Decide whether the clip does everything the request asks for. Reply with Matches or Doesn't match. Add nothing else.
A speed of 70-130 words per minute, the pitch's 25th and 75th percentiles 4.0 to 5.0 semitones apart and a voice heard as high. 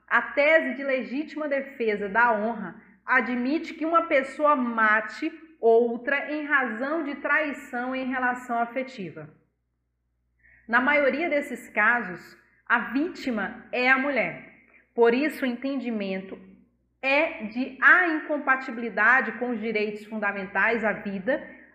Matches